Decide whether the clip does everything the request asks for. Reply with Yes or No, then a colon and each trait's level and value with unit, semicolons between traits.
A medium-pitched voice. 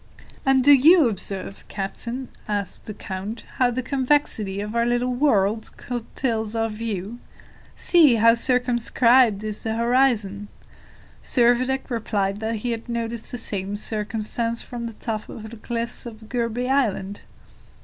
No: high, 230 Hz